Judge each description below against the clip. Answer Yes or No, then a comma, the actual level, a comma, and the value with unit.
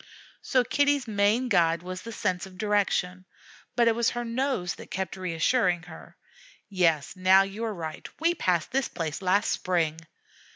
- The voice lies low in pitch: No, high, 190 Hz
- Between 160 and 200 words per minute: Yes, average, 165 wpm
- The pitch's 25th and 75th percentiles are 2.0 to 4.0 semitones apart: No, average, 4.6 semitones